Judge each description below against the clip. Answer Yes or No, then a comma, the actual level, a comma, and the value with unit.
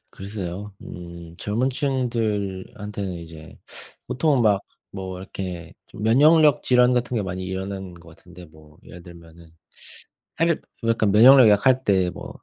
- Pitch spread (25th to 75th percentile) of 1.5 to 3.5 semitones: No, average, 5.1 semitones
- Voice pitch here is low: Yes, low, 100 Hz